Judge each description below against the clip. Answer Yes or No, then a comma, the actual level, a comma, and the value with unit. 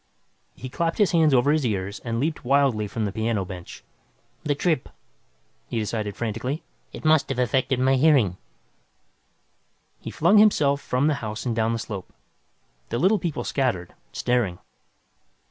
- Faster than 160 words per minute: No, average, 155 wpm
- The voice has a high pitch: No, low, 125 Hz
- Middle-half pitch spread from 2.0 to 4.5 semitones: No, average, 5.2 semitones